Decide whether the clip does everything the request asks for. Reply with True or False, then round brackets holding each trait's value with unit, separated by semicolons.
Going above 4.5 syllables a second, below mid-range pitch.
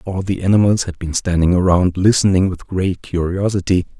True (5.3 syllables/s; 90 Hz)